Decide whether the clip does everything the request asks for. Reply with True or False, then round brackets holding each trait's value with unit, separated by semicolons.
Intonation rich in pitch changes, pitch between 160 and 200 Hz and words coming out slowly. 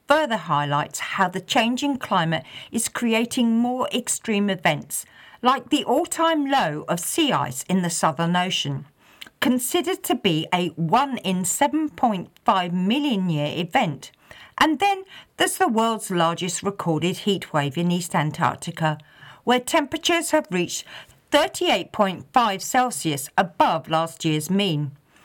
True (7.8 semitones; 190 Hz; 130 wpm)